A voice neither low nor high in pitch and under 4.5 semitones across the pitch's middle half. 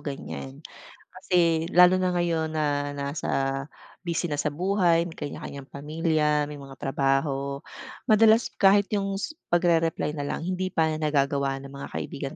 Yes: medium, 155 Hz; average, 3.9 semitones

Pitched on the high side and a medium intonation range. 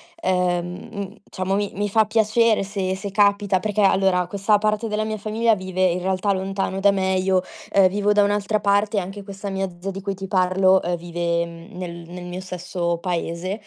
No: high, 195 Hz; narrow, 2.0 semitones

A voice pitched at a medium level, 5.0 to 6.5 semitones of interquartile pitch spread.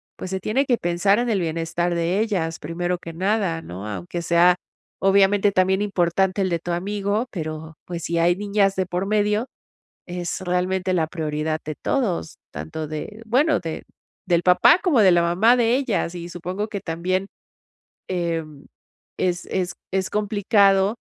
No: medium, 180 Hz; average, 3.2 semitones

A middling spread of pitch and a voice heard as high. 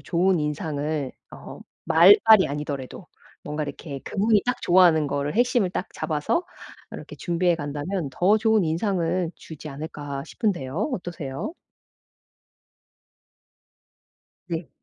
No: average, 4.5 semitones; medium, 165 Hz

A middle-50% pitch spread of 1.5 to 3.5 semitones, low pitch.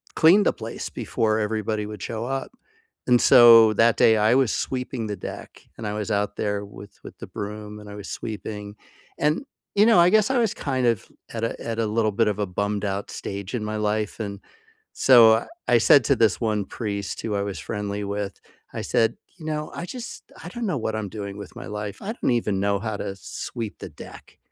Yes: average, 2.7 semitones; low, 110 Hz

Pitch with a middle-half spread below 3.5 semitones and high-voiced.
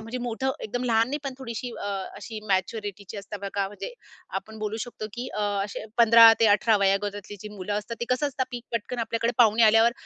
Yes: narrow, 2.5 semitones; high, 225 Hz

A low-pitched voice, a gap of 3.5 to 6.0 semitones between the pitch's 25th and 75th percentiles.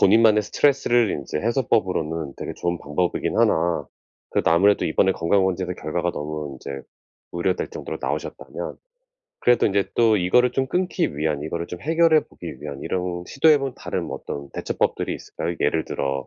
No: very low, 90 Hz; wide, 6.8 semitones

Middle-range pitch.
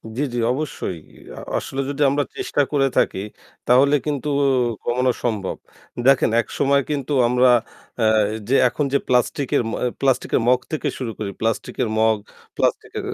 No: low, 130 Hz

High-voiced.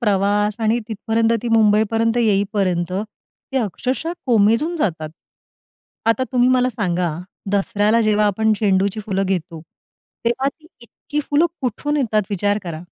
Yes: high, 215 Hz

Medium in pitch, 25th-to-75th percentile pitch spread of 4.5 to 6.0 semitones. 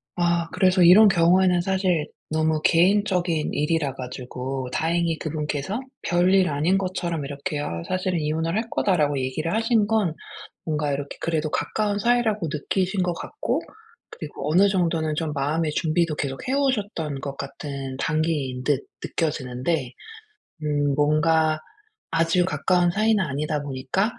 No: medium, 165 Hz; average, 4.1 semitones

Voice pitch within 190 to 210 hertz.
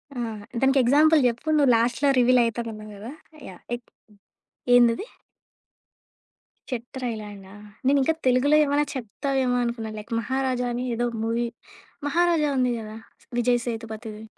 No: high, 245 Hz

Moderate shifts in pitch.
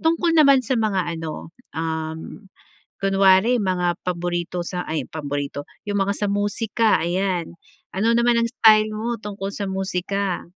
Yes: average, 3.9 semitones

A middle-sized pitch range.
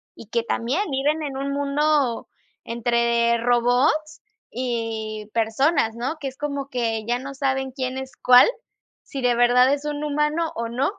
Yes: average, 3.3 semitones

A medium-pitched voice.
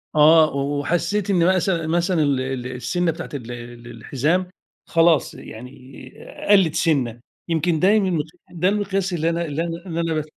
Yes: medium, 165 Hz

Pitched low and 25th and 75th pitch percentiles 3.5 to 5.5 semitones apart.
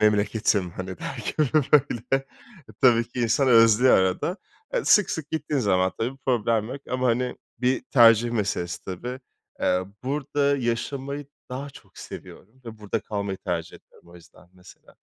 Yes: low, 115 Hz; average, 4.6 semitones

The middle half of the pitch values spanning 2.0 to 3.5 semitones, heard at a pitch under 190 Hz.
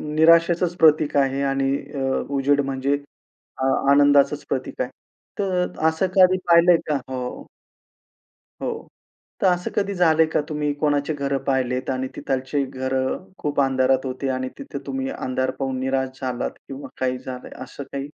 Yes: average, 3.2 semitones; medium, 140 Hz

